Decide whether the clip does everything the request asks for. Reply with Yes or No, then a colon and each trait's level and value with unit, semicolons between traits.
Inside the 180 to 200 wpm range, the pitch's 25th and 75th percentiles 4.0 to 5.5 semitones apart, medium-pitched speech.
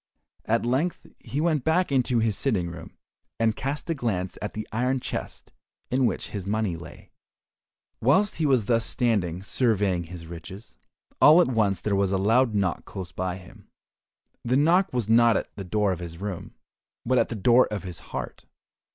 No: average, 185 wpm; average, 5.2 semitones; low, 110 Hz